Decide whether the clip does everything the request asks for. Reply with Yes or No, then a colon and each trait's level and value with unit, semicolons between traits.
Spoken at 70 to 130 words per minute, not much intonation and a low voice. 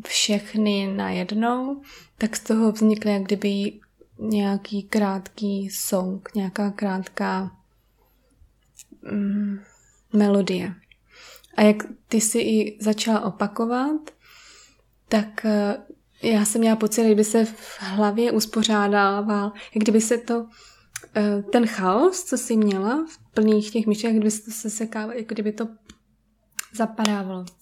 No: average, 120 wpm; narrow, 1.8 semitones; high, 215 Hz